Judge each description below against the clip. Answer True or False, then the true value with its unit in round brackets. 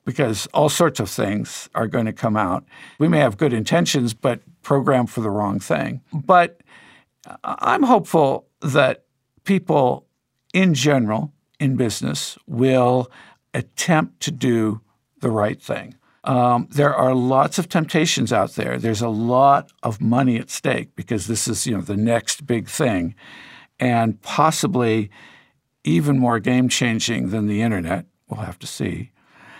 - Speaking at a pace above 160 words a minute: False (150 wpm)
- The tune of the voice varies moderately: True (3.7 semitones)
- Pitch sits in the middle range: False (120 Hz)